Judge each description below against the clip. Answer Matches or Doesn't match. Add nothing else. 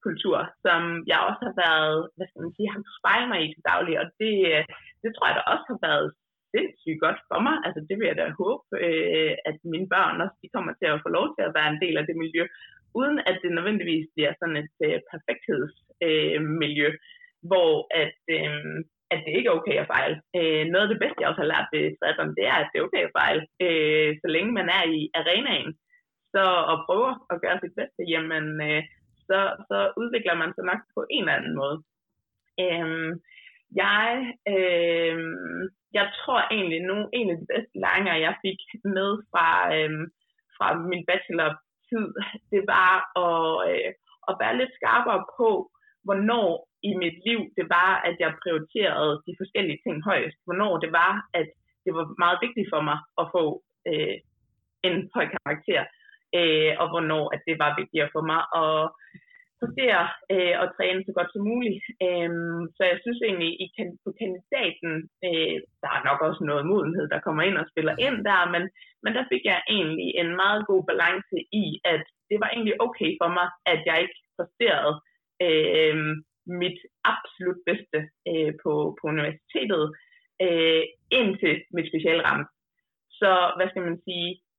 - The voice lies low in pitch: Doesn't match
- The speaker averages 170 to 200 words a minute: Matches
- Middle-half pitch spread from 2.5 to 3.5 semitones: Doesn't match